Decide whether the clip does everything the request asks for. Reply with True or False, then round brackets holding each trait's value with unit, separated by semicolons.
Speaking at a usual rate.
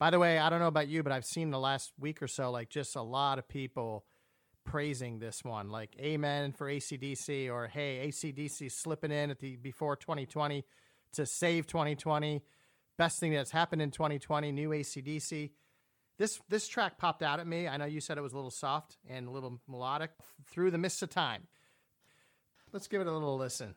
False (230 wpm)